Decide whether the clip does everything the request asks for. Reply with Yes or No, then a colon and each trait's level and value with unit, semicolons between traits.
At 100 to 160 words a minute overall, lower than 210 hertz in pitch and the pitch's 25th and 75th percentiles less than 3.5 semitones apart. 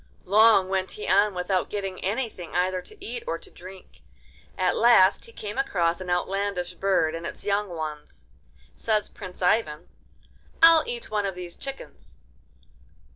Yes: average, 155 wpm; high, 190 Hz; average, 3.1 semitones